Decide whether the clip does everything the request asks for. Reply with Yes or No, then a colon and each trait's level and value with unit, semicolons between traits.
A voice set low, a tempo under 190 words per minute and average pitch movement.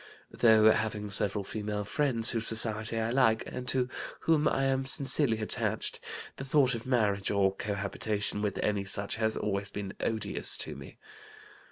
Yes: low, 110 Hz; average, 160 wpm; average, 3.3 semitones